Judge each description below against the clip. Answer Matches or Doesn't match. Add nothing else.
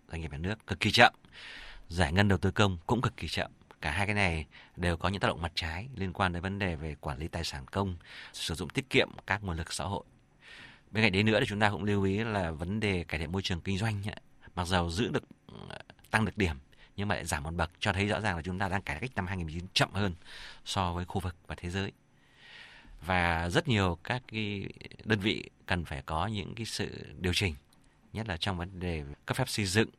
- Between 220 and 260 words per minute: Matches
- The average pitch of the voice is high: Doesn't match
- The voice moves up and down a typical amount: Matches